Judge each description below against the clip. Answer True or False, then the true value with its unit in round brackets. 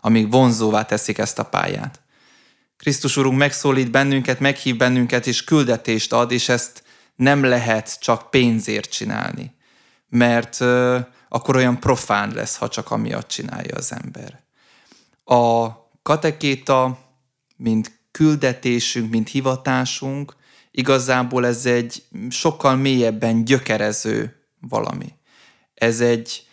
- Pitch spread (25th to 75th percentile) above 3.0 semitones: False (2.5 semitones)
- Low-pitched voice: True (125 Hz)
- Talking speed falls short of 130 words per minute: True (110 wpm)